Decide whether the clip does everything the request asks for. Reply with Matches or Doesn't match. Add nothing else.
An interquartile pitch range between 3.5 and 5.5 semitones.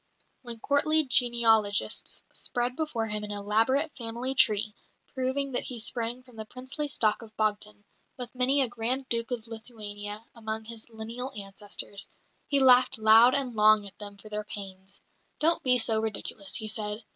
Doesn't match